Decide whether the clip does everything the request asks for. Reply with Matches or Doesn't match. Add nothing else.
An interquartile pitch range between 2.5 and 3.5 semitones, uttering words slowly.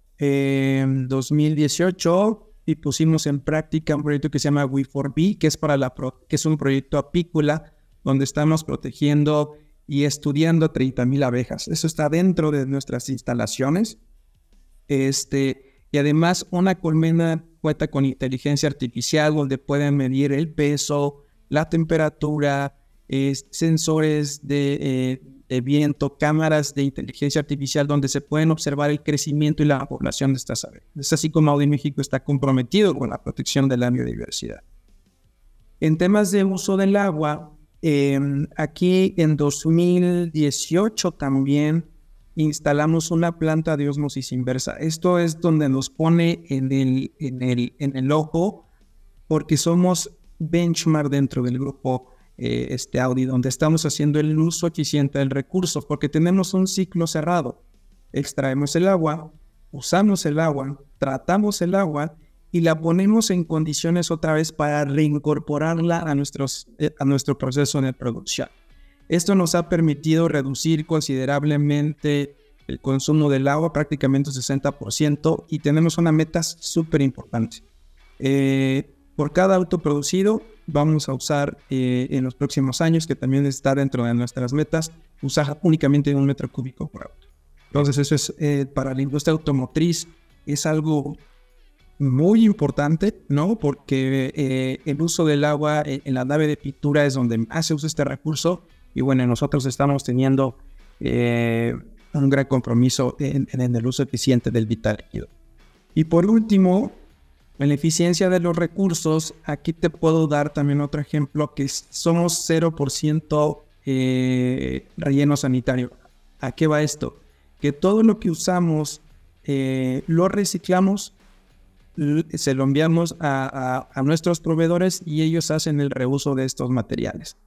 Doesn't match